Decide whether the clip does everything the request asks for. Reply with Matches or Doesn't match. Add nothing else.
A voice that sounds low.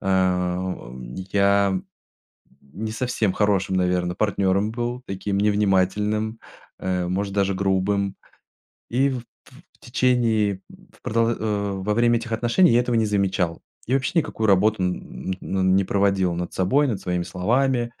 Matches